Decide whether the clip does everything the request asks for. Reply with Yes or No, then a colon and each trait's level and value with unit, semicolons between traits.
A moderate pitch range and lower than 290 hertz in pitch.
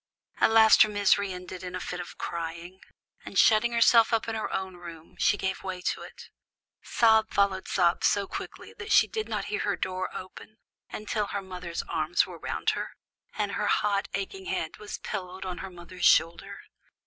Yes: average, 3.1 semitones; high, 190 Hz